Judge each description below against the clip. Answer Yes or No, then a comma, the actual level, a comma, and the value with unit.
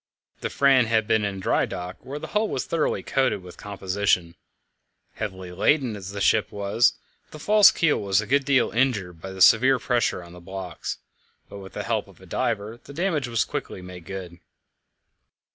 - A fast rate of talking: No, average, 190 wpm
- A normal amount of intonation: No, wide, 5.8 semitones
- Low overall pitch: Yes, low, 105 Hz